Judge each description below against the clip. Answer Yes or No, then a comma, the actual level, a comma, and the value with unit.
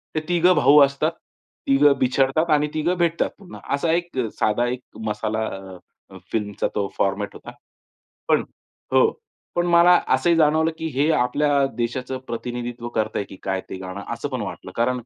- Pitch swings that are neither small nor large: No, wide, 6.2 semitones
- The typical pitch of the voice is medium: No, low, 130 Hz